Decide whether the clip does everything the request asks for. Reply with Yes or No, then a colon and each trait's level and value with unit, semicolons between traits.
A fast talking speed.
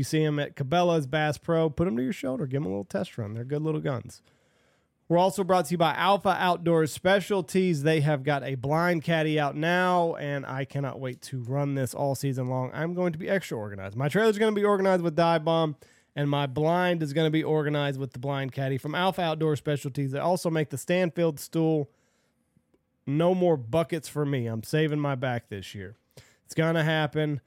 Yes: fast, 220 wpm